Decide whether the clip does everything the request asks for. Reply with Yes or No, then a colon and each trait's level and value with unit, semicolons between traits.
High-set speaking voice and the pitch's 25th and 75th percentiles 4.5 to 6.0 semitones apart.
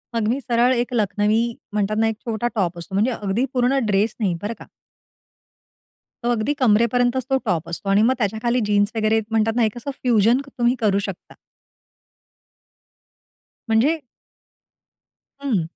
No: high, 225 Hz; average, 2.8 semitones